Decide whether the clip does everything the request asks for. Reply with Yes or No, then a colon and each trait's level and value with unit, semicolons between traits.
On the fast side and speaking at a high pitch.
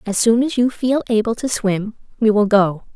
Yes: fast, 225 wpm; high, 220 Hz